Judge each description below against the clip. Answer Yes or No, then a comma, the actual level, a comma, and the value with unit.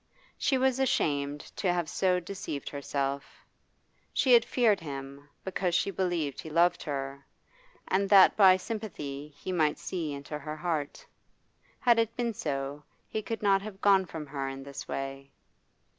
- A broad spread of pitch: Yes, wide, 5.8 semitones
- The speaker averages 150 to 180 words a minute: Yes, average, 160 wpm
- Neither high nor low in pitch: Yes, medium, 170 Hz